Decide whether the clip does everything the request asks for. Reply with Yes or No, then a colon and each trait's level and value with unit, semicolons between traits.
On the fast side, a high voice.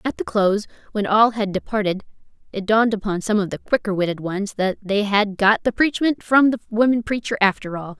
Yes: fast, 210 wpm; high, 210 Hz